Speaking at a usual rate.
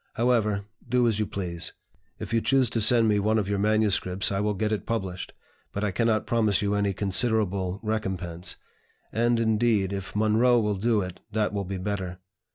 Yes: average, 185 wpm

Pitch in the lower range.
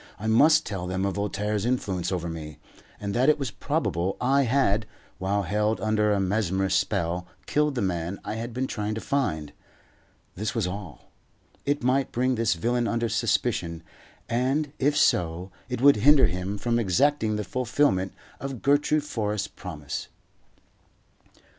Yes: low, 105 Hz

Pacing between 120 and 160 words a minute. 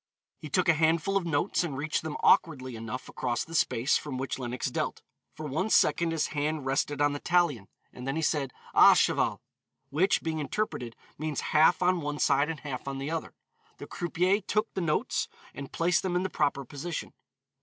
No: average, 195 wpm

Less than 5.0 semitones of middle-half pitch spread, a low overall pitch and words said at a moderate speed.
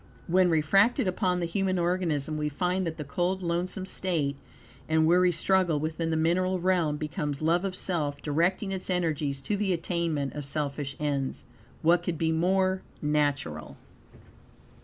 No: average, 3.6 semitones; medium, 170 Hz; average, 155 wpm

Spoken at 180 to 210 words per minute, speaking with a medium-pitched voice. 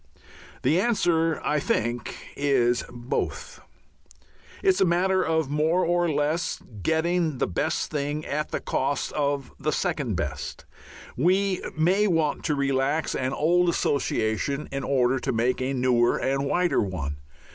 No: average, 145 wpm; medium, 145 Hz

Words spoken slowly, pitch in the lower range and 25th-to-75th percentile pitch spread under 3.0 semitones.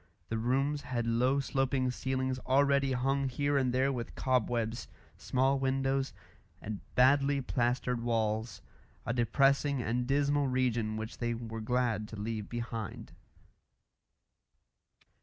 Yes: slow, 120 wpm; low, 125 Hz; narrow, 2.6 semitones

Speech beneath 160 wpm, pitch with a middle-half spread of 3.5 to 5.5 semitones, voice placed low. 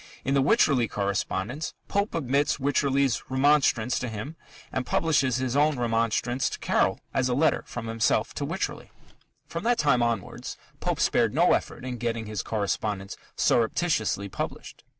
Yes: average, 150 wpm; average, 3.9 semitones; low, 125 Hz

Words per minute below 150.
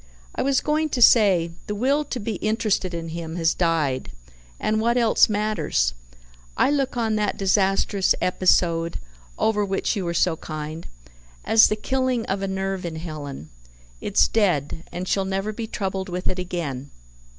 No: average, 165 wpm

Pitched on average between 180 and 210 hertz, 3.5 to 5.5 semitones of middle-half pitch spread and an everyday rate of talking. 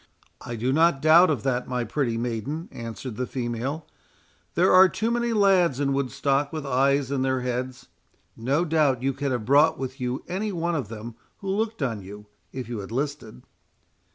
No: low, 135 Hz; average, 4.5 semitones; average, 180 wpm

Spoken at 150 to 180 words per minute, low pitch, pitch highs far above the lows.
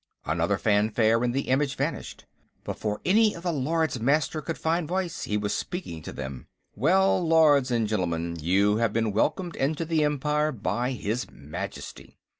Yes: average, 165 wpm; low, 130 Hz; wide, 7.3 semitones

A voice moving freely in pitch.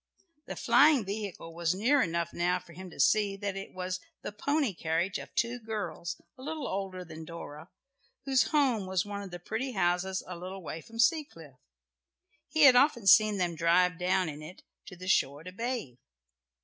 No: average, 4.6 semitones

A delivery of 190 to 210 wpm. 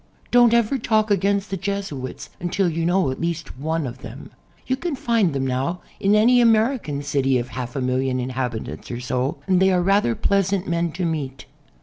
Yes: average, 195 wpm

